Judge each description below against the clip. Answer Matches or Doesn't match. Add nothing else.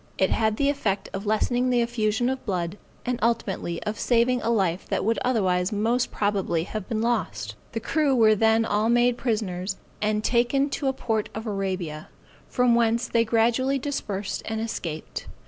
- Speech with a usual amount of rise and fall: Matches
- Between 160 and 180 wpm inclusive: Matches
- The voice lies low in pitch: Doesn't match